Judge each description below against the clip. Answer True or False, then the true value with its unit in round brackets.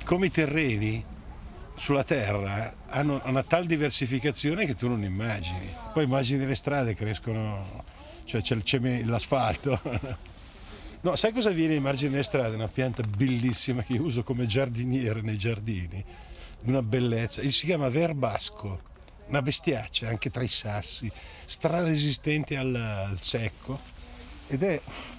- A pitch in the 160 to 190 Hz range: False (120 Hz)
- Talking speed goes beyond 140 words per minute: True (150 wpm)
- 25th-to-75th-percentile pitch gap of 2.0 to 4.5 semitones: False (5.0 semitones)